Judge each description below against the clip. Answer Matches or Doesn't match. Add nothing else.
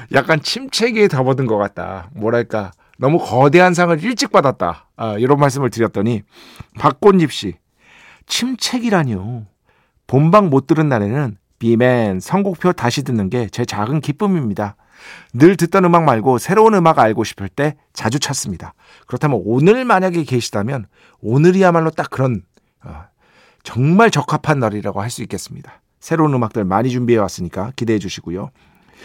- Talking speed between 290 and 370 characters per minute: Matches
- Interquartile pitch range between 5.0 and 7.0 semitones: Doesn't match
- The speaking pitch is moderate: Doesn't match